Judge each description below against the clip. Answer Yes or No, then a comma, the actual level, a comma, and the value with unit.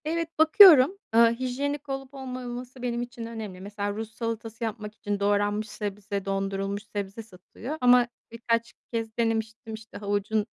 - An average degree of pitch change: Yes, average, 3.4 semitones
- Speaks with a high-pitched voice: Yes, high, 225 Hz